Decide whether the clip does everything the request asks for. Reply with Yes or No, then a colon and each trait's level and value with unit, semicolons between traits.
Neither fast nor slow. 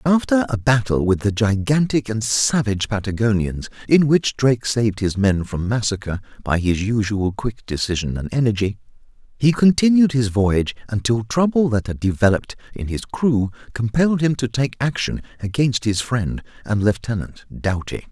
Yes: average, 155 wpm